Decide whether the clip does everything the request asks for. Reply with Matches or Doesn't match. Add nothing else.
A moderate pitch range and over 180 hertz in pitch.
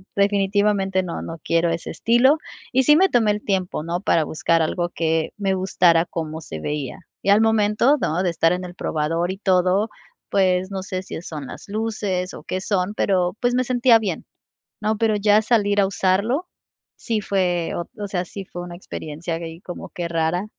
Matches